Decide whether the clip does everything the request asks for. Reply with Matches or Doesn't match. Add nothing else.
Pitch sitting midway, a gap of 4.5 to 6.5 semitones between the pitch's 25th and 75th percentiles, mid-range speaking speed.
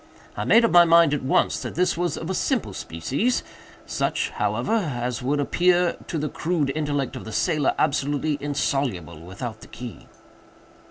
Matches